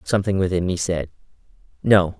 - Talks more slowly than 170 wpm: Yes, slow, 135 wpm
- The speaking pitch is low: Yes, very low, 95 Hz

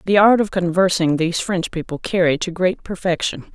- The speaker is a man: No, female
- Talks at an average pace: Yes, average, 185 wpm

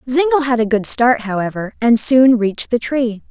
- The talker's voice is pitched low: No, high, 240 Hz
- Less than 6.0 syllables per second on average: Yes, 5.0 syllables/s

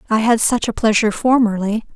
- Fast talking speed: No, average, 185 wpm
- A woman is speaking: Yes, female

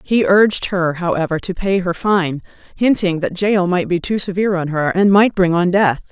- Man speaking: No, female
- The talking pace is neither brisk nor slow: No, fast, 215 wpm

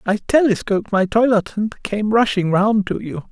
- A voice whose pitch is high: Yes, high, 210 Hz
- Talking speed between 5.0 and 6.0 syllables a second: No, 4.8 syllables/s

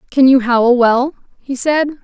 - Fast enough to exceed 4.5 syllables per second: No, 3.9 syllables/s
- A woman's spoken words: Yes, female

